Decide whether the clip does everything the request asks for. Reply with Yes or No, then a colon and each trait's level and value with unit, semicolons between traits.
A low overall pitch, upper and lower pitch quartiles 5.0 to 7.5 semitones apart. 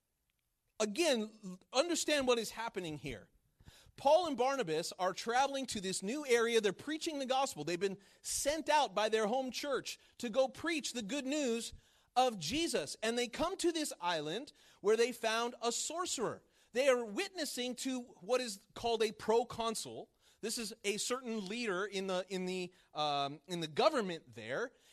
No: high, 230 Hz; wide, 5.5 semitones